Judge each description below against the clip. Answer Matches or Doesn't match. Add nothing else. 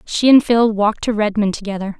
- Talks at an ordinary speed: Doesn't match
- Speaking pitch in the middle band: Doesn't match